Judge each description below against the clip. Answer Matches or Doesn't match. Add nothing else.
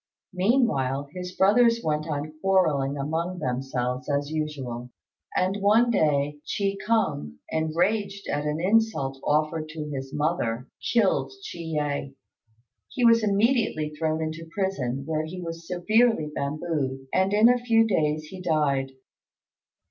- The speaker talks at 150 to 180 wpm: Doesn't match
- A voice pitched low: Doesn't match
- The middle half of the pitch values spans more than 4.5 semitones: Matches